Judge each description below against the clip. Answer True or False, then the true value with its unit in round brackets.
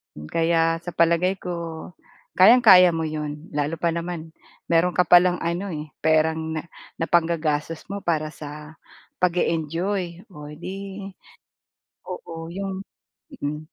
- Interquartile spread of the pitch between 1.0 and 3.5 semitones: True (2.4 semitones)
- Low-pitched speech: False (165 Hz)